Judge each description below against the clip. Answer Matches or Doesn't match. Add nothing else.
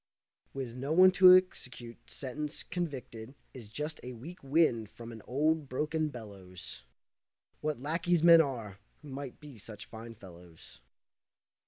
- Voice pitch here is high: Doesn't match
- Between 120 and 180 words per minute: Matches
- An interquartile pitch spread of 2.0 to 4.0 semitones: Doesn't match